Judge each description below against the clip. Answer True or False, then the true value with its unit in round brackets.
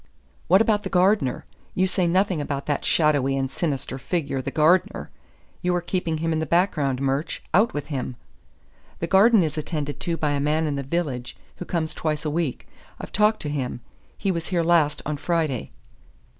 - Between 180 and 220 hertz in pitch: False (155 Hz)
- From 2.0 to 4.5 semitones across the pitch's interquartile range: True (3.9 semitones)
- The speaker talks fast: False (190 wpm)